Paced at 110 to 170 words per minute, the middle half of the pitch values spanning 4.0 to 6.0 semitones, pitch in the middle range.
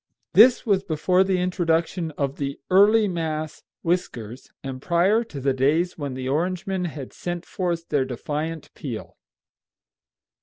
Yes: average, 140 wpm; average, 4.6 semitones; medium, 165 Hz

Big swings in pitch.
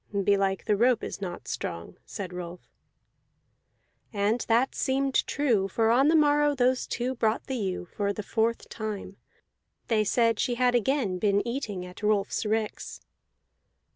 No: average, 4.0 semitones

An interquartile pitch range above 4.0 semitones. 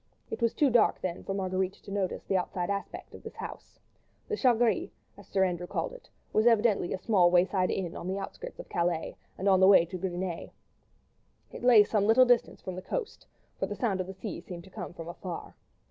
No: average, 3.5 semitones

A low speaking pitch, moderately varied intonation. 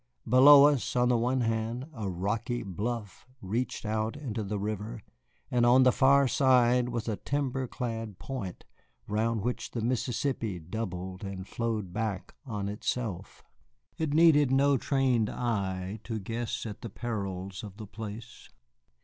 Yes: low, 115 Hz; average, 3.4 semitones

